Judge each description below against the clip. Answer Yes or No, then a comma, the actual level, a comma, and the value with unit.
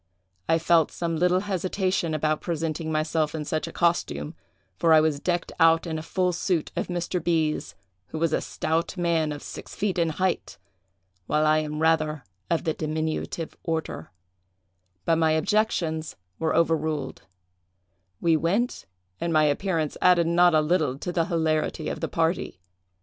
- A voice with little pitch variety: Yes, narrow, 1.8 semitones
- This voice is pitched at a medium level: Yes, medium, 160 Hz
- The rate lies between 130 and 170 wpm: Yes, average, 160 wpm